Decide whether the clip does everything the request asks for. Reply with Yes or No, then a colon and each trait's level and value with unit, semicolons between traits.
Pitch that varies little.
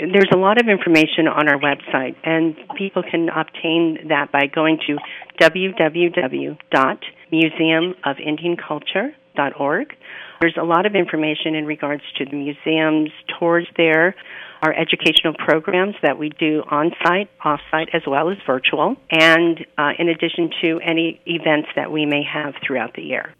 Yes: narrow, 2.0 semitones